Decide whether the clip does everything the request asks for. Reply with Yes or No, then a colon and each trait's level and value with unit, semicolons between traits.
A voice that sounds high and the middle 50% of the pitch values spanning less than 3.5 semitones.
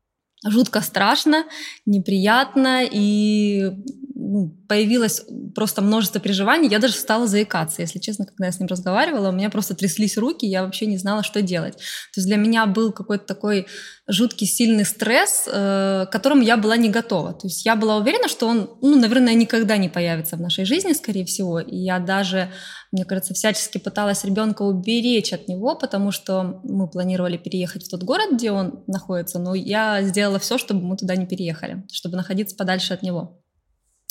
Yes: high, 205 Hz; average, 3.1 semitones